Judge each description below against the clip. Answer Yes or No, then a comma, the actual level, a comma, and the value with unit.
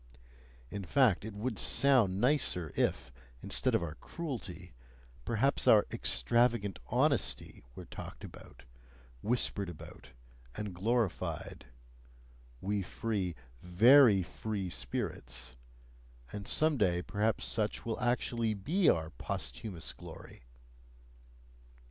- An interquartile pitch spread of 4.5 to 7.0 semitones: Yes, average, 5.1 semitones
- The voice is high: No, low, 105 Hz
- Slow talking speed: Yes, slow, 105 wpm